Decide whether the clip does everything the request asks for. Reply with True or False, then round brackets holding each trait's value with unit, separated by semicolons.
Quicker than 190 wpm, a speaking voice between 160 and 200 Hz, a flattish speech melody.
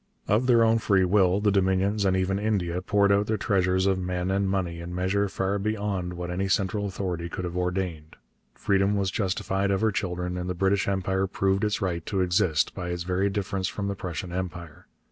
False (205 wpm; 95 Hz; 1.9 semitones)